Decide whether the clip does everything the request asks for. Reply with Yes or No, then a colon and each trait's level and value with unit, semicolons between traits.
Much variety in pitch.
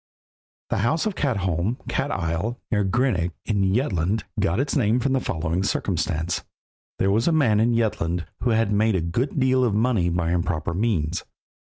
Yes: wide, 5.7 semitones